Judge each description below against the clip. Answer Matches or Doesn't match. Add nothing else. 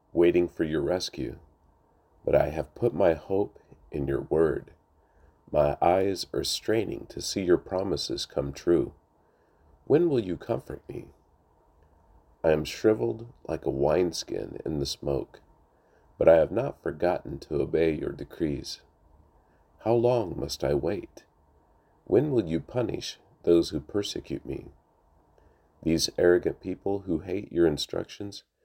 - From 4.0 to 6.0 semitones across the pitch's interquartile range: Matches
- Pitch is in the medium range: Doesn't match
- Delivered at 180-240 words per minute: Doesn't match